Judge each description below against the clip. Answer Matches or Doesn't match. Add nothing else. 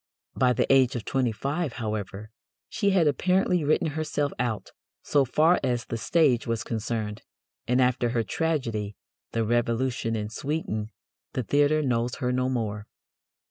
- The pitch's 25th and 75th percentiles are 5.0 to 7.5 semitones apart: Doesn't match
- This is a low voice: Matches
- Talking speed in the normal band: Matches